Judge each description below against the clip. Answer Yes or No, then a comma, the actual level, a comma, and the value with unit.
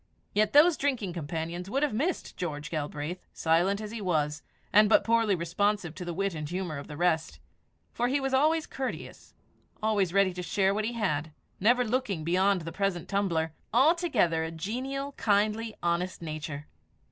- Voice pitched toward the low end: No, high, 195 Hz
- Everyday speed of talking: Yes, average, 170 wpm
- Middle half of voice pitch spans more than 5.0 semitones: Yes, wide, 5.4 semitones